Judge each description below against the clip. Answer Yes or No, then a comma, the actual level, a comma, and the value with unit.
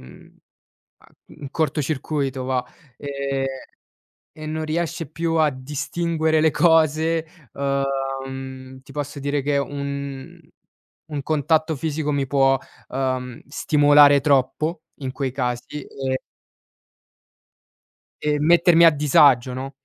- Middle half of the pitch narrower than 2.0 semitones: No, narrow, 2.6 semitones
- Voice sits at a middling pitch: Yes, medium, 145 Hz